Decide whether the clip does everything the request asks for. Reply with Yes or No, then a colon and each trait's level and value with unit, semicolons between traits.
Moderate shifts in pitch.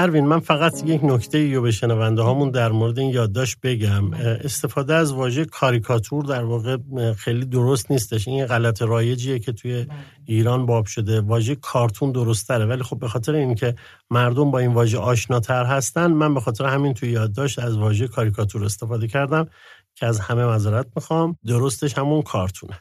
Yes: average, 3.3 semitones